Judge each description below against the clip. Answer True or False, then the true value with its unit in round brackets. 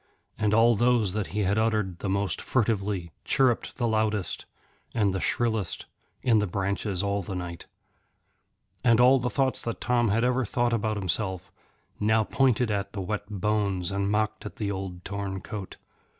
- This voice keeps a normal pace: True (170 wpm)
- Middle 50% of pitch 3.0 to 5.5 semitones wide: False (2.6 semitones)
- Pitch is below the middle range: True (105 Hz)